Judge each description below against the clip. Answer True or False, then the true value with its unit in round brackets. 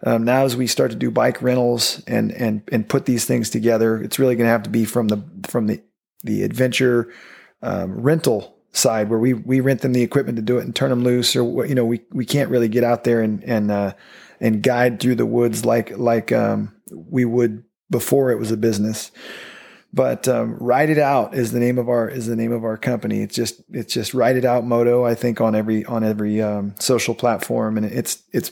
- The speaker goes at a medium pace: False (235 wpm)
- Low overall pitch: True (120 Hz)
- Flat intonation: True (1.7 semitones)